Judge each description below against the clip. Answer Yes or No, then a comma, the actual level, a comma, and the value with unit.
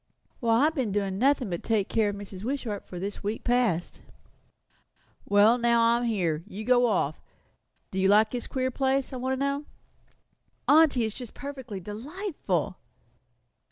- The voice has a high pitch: Yes, high, 230 Hz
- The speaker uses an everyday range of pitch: Yes, average, 4.4 semitones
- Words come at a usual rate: Yes, average, 165 wpm